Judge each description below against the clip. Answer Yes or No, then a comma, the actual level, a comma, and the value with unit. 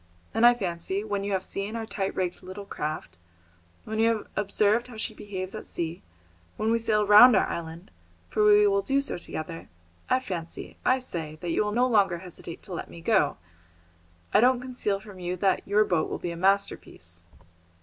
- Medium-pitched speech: No, high, 200 Hz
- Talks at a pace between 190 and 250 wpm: Yes, average, 200 wpm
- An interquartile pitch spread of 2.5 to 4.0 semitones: Yes, average, 3.7 semitones